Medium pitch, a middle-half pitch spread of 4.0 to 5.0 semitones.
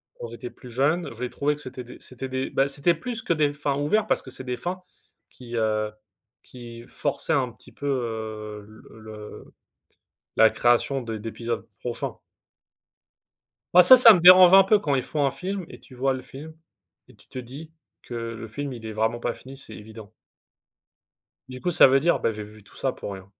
No: low, 130 Hz; average, 4.6 semitones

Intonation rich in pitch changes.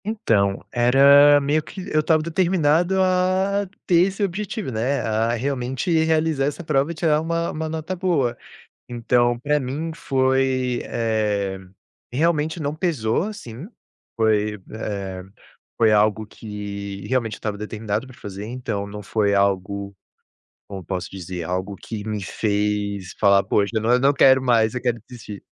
Yes: wide, 6.9 semitones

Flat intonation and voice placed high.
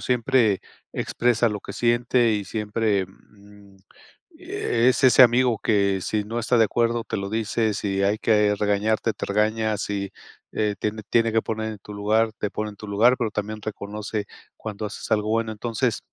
No: narrow, 1.9 semitones; low, 110 Hz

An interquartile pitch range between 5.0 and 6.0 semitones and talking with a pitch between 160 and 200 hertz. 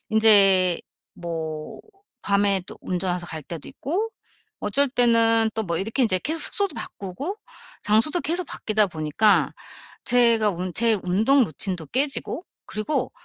No: average, 5.3 semitones; high, 215 Hz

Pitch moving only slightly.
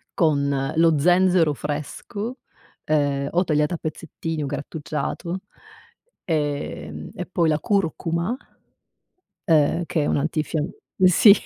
No: average, 3.1 semitones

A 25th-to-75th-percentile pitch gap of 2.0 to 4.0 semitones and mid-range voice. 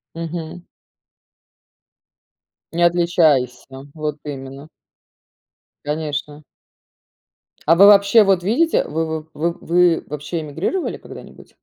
Yes: average, 2.9 semitones; medium, 165 Hz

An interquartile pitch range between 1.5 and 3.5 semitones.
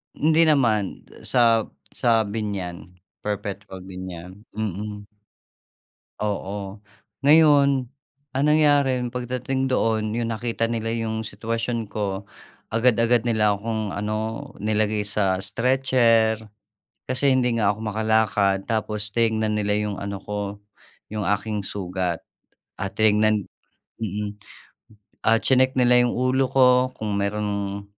Yes: average, 2.8 semitones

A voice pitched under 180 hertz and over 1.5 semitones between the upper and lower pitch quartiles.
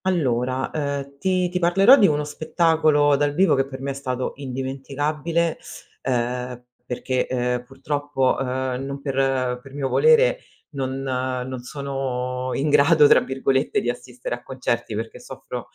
Yes: low, 135 Hz; narrow, 2.6 semitones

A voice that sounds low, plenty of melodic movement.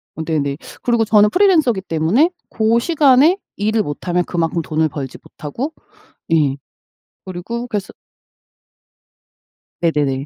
No: high, 190 Hz; wide, 7.1 semitones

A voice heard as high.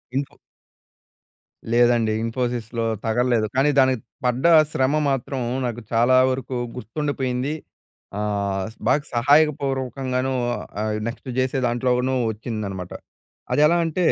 No: low, 125 Hz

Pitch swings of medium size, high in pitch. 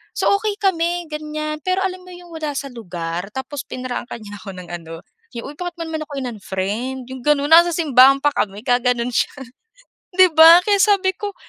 No: wide, 6.0 semitones; very high, 290 Hz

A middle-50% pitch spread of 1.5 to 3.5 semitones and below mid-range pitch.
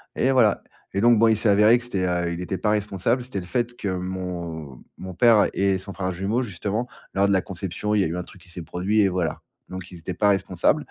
Yes: average, 3.0 semitones; very low, 95 Hz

